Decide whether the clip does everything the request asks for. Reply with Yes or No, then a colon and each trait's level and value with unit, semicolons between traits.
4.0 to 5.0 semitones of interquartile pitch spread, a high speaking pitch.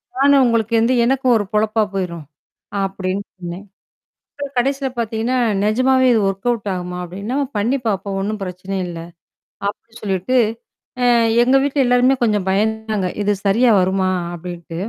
Yes: average, 4.4 semitones; high, 215 Hz